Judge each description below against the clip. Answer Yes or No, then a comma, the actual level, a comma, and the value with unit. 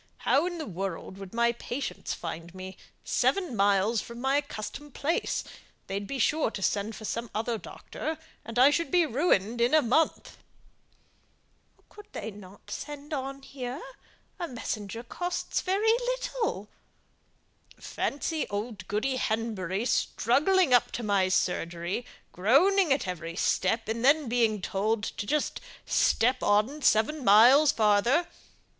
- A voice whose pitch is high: Yes, high, 235 Hz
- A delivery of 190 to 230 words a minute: No, average, 140 wpm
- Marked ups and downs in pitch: Yes, wide, 6.1 semitones